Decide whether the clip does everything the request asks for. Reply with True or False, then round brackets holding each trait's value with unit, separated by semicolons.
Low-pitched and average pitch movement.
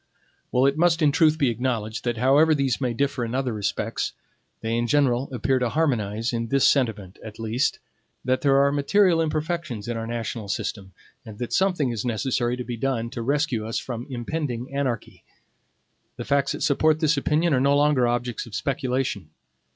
True (130 Hz; 3.5 semitones)